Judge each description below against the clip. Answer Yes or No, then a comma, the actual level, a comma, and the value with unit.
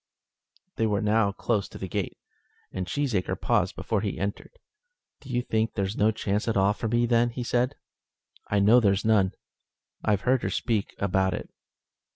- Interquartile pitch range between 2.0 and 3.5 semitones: Yes, average, 3.1 semitones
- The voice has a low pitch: Yes, low, 105 Hz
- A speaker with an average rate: Yes, average, 180 wpm